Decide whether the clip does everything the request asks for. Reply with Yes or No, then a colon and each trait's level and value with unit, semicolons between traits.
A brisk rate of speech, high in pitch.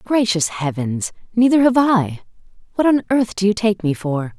No: average, 180 wpm; high, 200 Hz